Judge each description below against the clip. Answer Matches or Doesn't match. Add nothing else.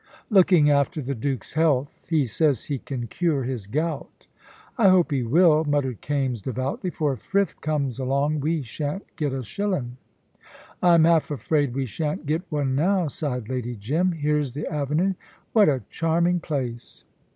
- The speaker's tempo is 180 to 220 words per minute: Doesn't match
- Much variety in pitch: Doesn't match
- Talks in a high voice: Doesn't match